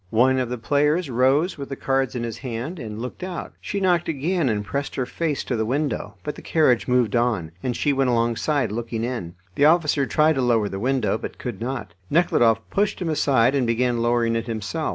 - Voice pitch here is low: Yes, low, 125 Hz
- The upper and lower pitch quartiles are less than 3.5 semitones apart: No, average, 4.1 semitones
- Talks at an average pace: No, fast, 215 wpm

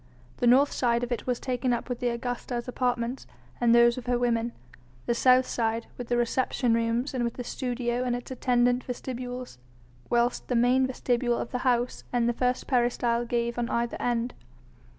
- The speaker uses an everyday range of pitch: No, narrow, 0.9 semitones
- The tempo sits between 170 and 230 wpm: Yes, average, 190 wpm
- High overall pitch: Yes, high, 245 Hz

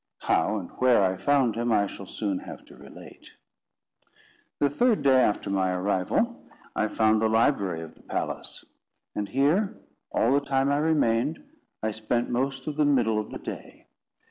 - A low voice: Yes, low, 120 Hz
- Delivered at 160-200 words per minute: Yes, average, 170 wpm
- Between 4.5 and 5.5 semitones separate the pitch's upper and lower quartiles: Yes, average, 5.2 semitones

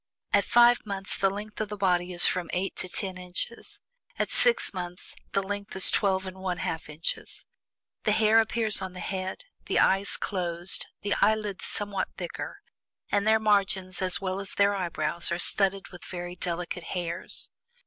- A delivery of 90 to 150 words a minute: No, average, 175 wpm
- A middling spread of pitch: No, narrow, 2.2 semitones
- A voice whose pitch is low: No, high, 190 Hz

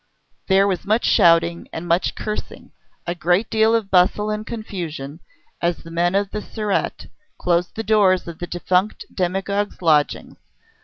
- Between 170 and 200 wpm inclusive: No, average, 155 wpm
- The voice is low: No, medium, 185 Hz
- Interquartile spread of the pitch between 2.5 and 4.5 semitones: Yes, average, 3.4 semitones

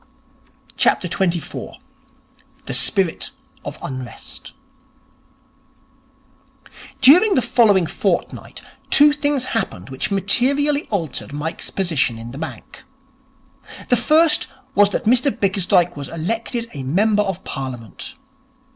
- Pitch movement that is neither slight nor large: No, wide, 8.0 semitones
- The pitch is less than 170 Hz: No, high, 195 Hz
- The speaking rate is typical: No, slow, 100 wpm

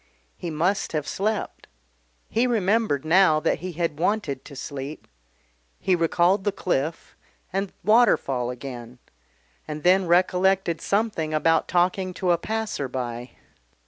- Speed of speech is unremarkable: No, slow, 130 wpm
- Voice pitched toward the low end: No, medium, 175 Hz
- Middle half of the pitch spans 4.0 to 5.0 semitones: Yes, average, 4.5 semitones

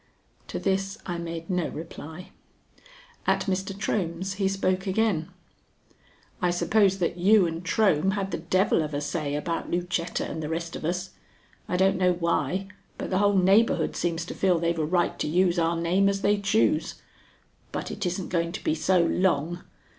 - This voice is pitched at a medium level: Yes, medium, 180 Hz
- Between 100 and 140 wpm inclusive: No, average, 180 wpm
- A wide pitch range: No, narrow, 2.4 semitones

